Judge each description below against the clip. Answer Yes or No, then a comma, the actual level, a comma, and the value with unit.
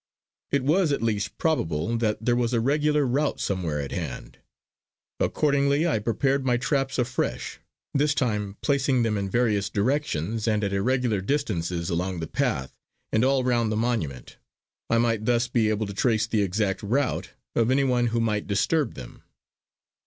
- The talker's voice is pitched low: Yes, low, 115 Hz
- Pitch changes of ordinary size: Yes, average, 4.7 semitones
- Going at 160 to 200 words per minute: Yes, average, 165 wpm